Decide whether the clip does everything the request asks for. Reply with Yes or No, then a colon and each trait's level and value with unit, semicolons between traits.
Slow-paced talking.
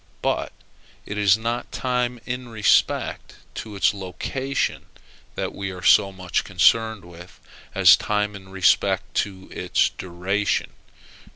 Yes: slow, 125 wpm